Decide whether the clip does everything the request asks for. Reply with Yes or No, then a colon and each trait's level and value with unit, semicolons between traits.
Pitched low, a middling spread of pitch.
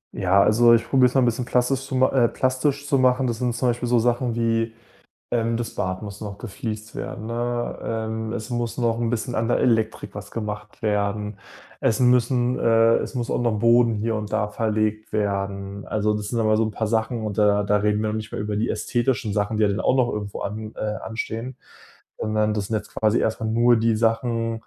No: low, 115 Hz; narrow, 2.1 semitones